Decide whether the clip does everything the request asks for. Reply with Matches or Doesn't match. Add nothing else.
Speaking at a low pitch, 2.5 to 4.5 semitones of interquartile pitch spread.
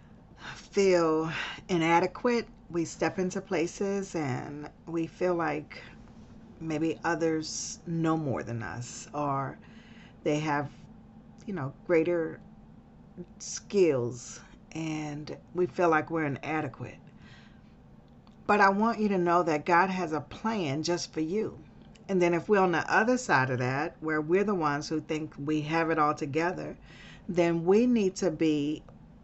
Doesn't match